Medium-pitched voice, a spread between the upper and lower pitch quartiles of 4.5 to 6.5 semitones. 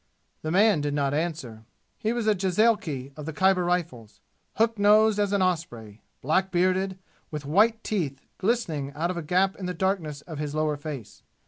Yes: medium, 175 Hz; average, 5.0 semitones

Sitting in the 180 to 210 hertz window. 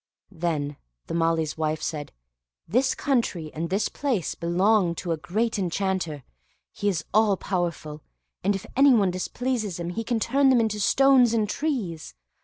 Yes: high, 190 Hz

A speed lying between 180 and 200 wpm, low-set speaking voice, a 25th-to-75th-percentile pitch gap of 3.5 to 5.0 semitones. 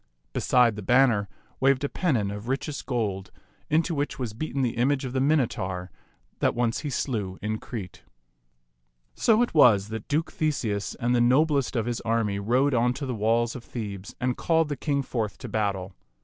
Yes: average, 185 wpm; low, 120 Hz; average, 4.6 semitones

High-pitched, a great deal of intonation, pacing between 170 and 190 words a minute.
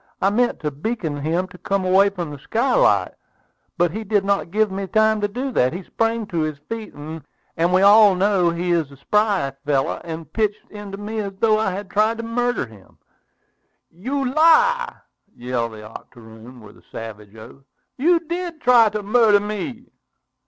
Yes: high, 200 Hz; wide, 5.9 semitones; average, 180 wpm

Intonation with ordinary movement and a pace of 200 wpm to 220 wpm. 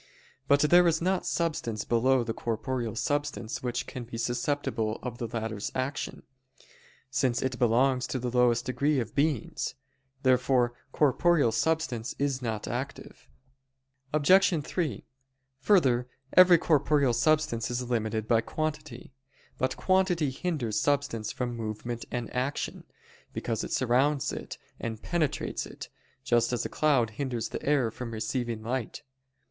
No: average, 3.8 semitones; slow, 135 wpm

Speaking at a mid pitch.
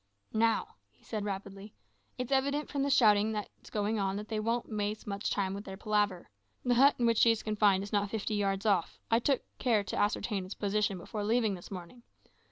No: high, 210 Hz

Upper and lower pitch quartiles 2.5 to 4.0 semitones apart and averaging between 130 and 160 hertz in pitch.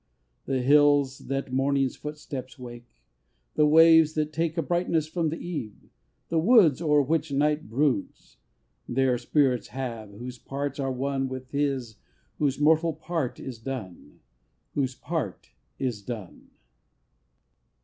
Yes: average, 3.3 semitones; medium, 140 Hz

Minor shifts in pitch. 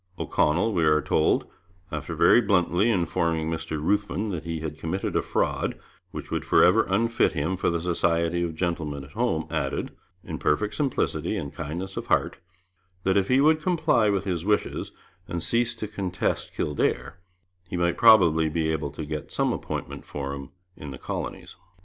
No: average, 4.4 semitones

